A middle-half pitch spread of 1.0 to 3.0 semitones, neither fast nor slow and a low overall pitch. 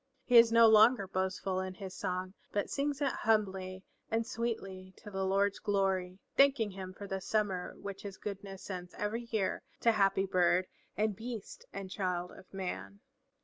No: average, 2.7 semitones; average, 170 wpm; high, 195 Hz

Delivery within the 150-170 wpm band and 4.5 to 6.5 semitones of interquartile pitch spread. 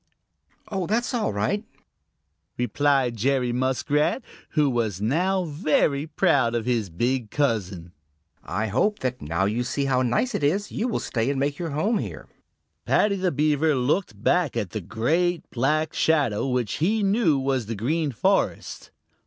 Yes: average, 160 wpm; wide, 5.6 semitones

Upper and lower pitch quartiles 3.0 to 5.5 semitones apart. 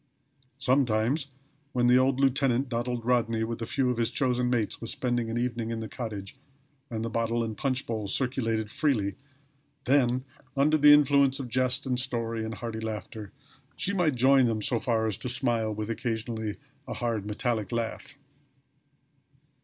No: narrow, 2.5 semitones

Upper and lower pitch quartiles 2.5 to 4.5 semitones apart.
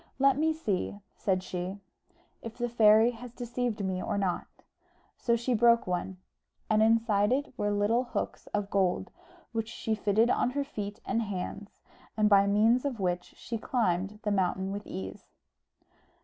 Yes: average, 3.2 semitones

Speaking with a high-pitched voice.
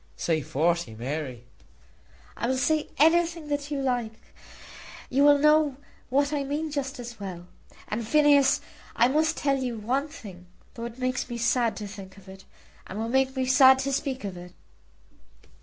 Yes: very high, 255 Hz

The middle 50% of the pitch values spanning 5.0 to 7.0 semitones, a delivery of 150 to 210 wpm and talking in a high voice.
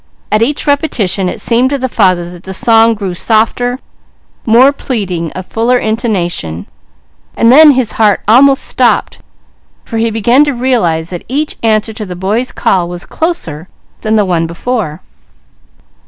Yes: average, 5.3 semitones; average, 155 wpm; high, 220 Hz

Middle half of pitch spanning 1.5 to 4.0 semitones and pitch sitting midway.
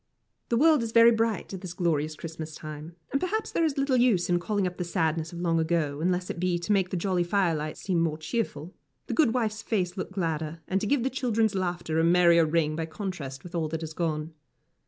No: average, 4.8 semitones; medium, 175 Hz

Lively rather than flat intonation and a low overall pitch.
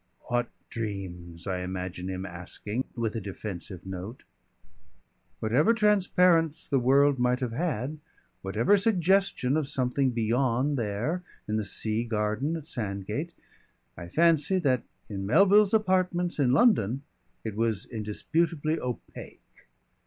Yes: wide, 7.5 semitones; low, 125 Hz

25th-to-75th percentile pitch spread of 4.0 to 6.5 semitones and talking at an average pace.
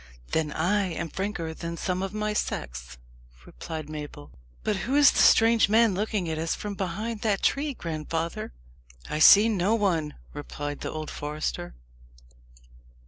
Yes: average, 5.3 semitones; average, 150 wpm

